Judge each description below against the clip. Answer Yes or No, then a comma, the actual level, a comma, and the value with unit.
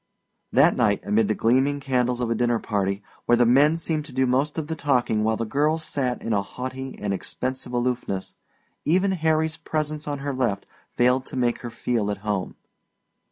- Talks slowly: No, average, 195 wpm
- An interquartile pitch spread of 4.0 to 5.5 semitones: Yes, average, 4.3 semitones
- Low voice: Yes, low, 125 Hz